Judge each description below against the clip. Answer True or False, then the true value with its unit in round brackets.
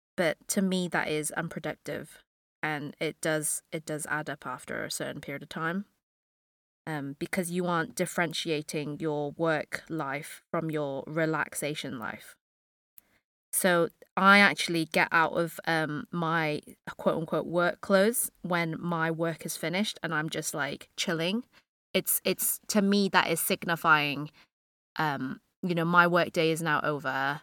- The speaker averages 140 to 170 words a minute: True (150 wpm)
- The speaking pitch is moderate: True (160 Hz)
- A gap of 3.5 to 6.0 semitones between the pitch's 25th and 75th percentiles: False (2.6 semitones)